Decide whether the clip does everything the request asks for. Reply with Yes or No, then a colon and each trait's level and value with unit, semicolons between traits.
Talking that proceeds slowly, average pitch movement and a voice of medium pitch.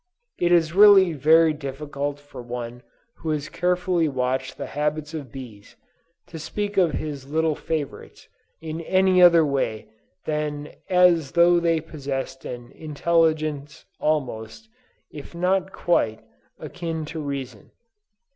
Yes: slow, 125 wpm; average, 3.6 semitones; medium, 155 Hz